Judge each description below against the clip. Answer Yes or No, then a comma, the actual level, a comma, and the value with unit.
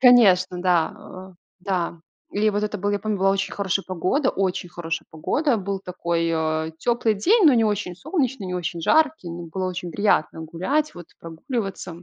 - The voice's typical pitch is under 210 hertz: Yes, high, 190 Hz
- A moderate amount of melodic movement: Yes, average, 3.9 semitones